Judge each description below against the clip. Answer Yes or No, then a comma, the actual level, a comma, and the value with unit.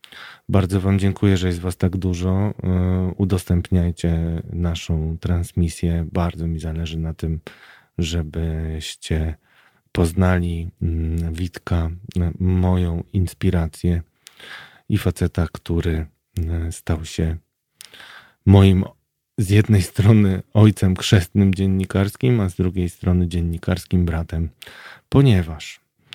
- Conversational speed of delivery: No, slow, 90 wpm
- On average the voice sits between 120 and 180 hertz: No, very low, 90 Hz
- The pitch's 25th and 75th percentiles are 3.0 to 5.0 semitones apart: No, narrow, 2.4 semitones